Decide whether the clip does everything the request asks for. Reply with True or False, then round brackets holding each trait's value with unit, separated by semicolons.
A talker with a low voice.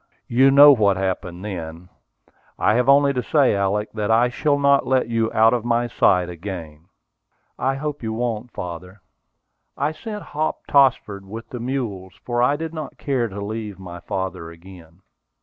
True (110 Hz)